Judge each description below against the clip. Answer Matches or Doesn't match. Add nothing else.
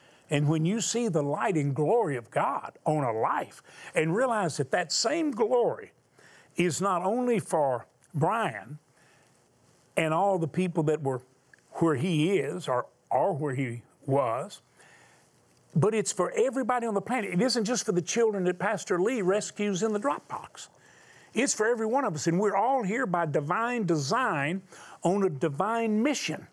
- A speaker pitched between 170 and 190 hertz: Matches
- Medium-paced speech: Matches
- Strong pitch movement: Matches